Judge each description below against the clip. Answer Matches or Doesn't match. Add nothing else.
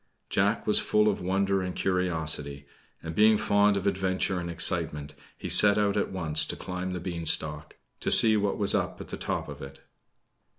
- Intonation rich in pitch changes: Doesn't match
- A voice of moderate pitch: Doesn't match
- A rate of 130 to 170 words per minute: Doesn't match